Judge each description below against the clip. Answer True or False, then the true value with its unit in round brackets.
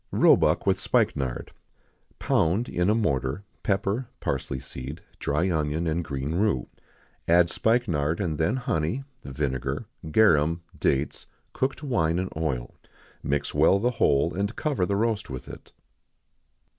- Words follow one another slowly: True (130 wpm)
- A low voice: True (85 Hz)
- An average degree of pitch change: False (6.2 semitones)